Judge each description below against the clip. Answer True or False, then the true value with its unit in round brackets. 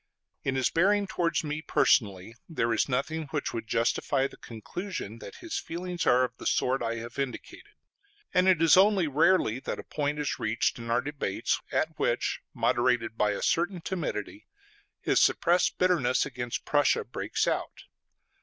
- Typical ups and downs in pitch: False (6.5 semitones)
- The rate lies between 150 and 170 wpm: True (165 wpm)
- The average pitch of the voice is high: False (140 Hz)